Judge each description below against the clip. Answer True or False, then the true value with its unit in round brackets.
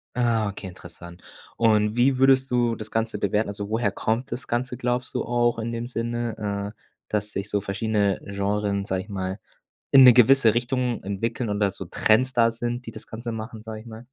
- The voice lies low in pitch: True (115 Hz)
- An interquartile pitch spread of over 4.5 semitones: False (2.8 semitones)